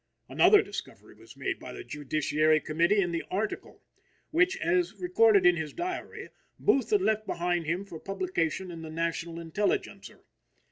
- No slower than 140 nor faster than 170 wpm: Yes, average, 155 wpm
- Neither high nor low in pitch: Yes, medium, 180 Hz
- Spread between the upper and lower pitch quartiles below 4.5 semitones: No, wide, 5.5 semitones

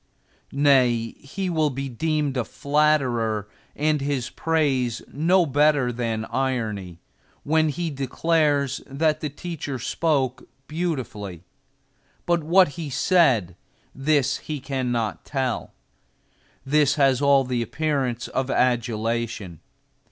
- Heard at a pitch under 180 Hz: Yes, low, 135 Hz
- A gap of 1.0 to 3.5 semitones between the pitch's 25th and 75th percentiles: No, average, 4.0 semitones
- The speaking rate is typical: No, slow, 110 wpm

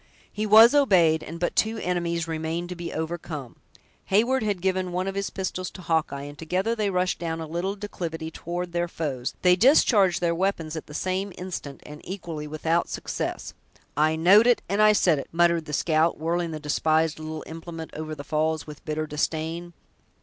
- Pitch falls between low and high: Yes, medium, 170 Hz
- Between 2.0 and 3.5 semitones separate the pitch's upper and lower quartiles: Yes, average, 2.9 semitones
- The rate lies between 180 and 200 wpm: Yes, average, 190 wpm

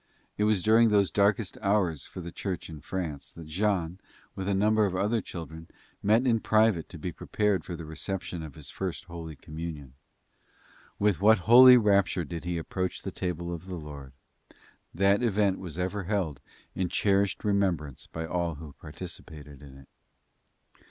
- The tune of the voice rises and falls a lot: No, average, 3.9 semitones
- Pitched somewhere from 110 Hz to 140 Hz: No, very low, 90 Hz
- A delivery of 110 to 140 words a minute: No, average, 170 wpm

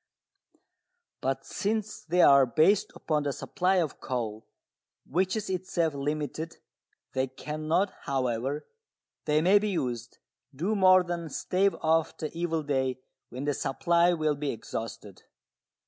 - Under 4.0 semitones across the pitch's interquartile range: No, average, 5.2 semitones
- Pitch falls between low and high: Yes, medium, 155 Hz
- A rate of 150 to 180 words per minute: No, slow, 135 wpm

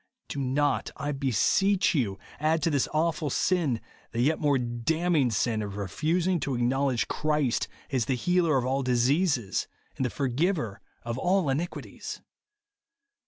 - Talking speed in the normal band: Yes, average, 155 wpm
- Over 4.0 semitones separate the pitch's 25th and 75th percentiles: Yes, average, 4.8 semitones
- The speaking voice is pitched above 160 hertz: No, medium, 140 Hz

